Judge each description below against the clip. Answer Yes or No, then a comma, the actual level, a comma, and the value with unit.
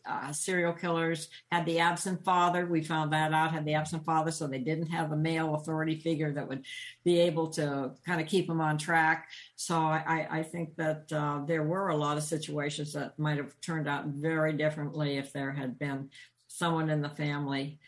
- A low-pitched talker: No, medium, 155 Hz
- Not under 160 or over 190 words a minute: No, fast, 205 wpm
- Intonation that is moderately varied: No, narrow, 2.0 semitones